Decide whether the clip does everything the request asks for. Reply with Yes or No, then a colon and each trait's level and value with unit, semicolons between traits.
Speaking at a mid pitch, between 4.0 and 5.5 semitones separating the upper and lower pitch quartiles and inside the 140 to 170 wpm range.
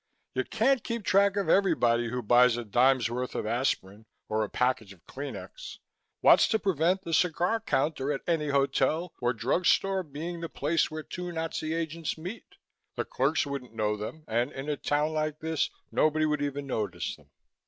No: medium, 150 Hz; average, 5.0 semitones; average, 185 wpm